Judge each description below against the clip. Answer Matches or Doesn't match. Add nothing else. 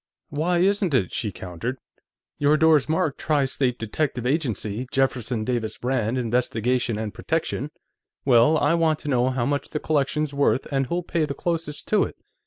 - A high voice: Doesn't match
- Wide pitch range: Doesn't match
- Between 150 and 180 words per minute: Matches